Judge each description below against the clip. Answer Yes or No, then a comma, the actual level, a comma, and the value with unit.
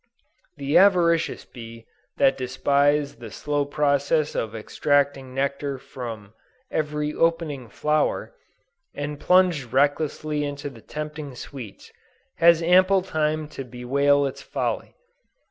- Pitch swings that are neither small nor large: No, narrow, 2.3 semitones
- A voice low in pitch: No, medium, 145 Hz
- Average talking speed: No, slow, 110 wpm